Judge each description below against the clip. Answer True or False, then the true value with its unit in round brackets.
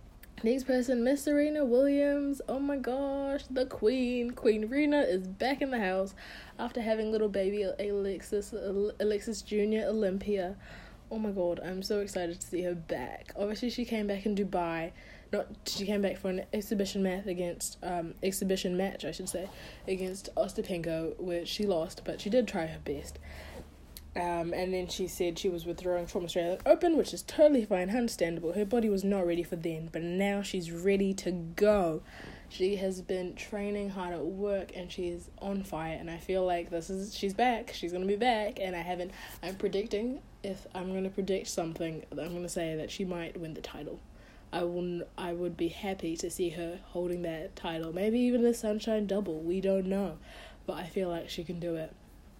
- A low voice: False (190 Hz)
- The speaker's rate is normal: True (195 wpm)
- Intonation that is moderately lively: True (3.4 semitones)